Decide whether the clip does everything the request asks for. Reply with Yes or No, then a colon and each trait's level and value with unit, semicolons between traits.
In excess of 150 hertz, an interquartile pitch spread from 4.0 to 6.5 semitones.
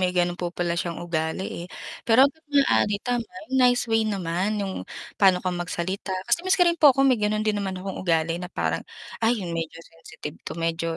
Yes: high, 190 Hz; average, 5.3 semitones